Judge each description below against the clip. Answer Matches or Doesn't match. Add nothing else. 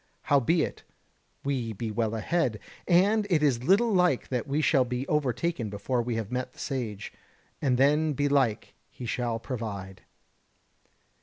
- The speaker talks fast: Doesn't match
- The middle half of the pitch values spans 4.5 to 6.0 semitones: Matches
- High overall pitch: Doesn't match